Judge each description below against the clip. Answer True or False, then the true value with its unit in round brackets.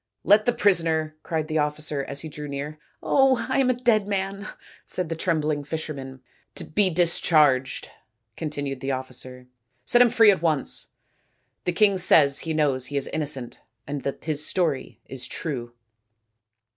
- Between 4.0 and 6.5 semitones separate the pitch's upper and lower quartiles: True (4.8 semitones)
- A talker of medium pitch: True (155 Hz)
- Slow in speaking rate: False (170 wpm)